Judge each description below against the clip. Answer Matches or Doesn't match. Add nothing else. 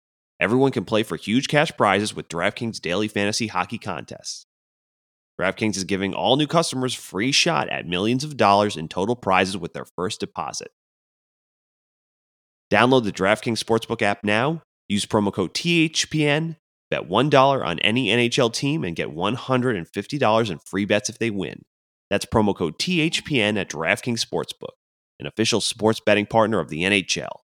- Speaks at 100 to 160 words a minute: Matches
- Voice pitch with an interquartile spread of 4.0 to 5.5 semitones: Matches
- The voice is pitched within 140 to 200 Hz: Doesn't match